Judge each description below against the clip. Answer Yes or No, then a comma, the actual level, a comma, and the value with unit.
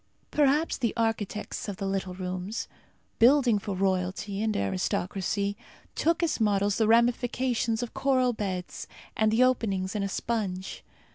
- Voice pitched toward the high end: Yes, high, 210 Hz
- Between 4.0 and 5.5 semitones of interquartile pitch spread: No, average, 3.6 semitones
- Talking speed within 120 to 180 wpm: Yes, average, 140 wpm